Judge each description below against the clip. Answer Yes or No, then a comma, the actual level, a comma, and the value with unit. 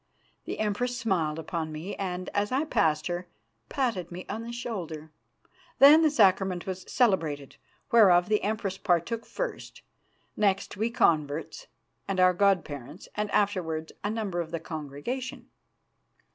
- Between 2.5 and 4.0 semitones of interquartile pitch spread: No, average, 5.2 semitones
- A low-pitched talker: No, high, 190 Hz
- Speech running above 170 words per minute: No, average, 145 wpm